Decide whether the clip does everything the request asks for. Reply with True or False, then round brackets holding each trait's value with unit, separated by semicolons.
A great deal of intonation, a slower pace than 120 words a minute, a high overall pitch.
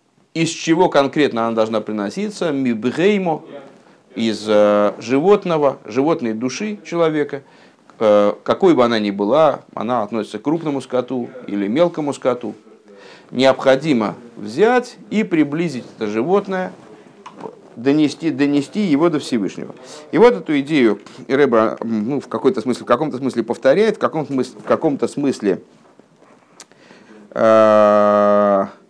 False (6.8 semitones; 110 wpm; 135 Hz)